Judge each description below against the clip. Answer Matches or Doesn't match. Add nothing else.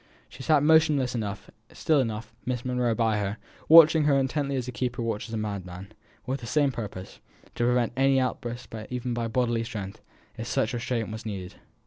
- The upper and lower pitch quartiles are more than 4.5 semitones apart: Doesn't match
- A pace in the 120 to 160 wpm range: Doesn't match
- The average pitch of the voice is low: Matches